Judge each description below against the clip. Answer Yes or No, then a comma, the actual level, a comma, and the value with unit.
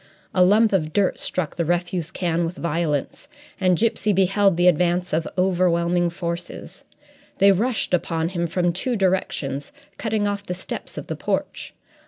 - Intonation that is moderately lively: No, narrow, 2.3 semitones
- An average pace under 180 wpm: Yes, average, 160 wpm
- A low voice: No, medium, 180 Hz